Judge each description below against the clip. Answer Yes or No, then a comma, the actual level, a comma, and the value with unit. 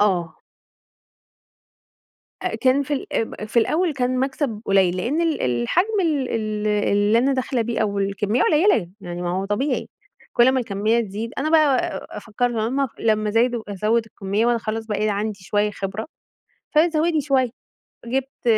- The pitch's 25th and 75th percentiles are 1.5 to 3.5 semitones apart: No, average, 4.4 semitones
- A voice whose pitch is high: Yes, high, 225 Hz